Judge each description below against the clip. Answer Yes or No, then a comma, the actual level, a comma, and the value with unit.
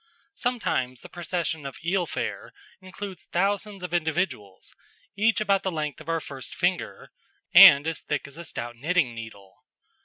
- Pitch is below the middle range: No, medium, 165 Hz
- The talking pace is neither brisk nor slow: Yes, average, 155 wpm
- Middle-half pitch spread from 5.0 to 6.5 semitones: Yes, wide, 5.5 semitones